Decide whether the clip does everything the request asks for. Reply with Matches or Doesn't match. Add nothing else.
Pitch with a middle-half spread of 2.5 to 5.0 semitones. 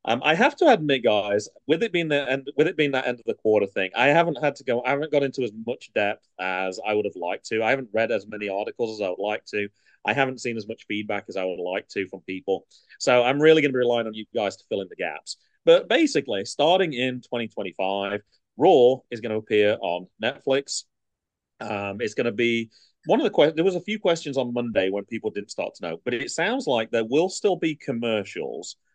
Doesn't match